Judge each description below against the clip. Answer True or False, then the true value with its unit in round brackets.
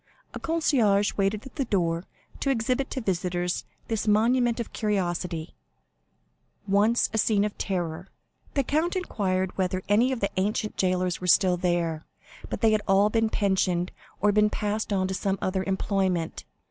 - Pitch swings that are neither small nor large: True (3.3 semitones)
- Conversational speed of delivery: True (160 wpm)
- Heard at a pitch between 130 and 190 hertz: False (200 Hz)